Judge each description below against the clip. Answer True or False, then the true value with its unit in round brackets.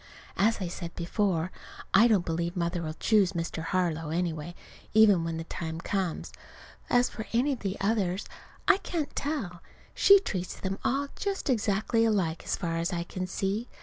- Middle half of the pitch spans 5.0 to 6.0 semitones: False (4.6 semitones)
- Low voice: False (190 Hz)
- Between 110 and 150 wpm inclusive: False (170 wpm)